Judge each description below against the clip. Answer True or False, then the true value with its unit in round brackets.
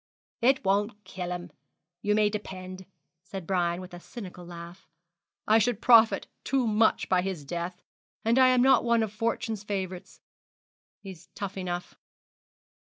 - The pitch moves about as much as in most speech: True (3.7 semitones)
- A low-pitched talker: False (195 Hz)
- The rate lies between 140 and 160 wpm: True (145 wpm)